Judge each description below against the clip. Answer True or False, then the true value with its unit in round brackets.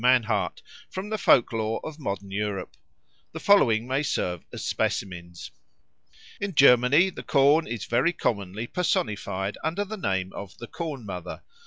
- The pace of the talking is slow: False (150 wpm)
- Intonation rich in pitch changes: True (7.6 semitones)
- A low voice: True (120 Hz)